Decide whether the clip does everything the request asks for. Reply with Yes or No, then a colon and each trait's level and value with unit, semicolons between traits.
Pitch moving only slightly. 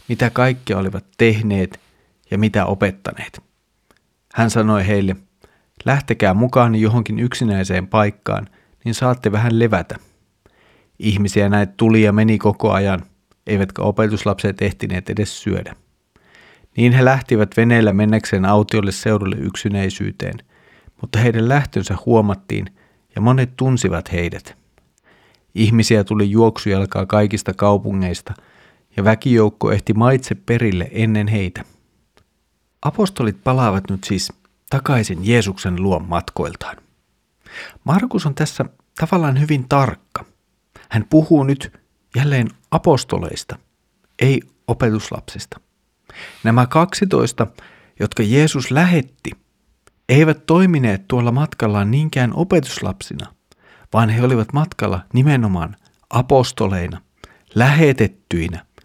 No: average, 3.9 semitones